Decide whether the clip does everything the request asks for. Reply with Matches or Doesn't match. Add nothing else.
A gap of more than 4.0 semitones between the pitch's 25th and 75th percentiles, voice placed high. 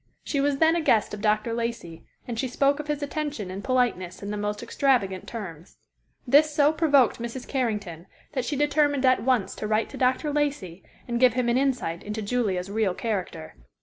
Matches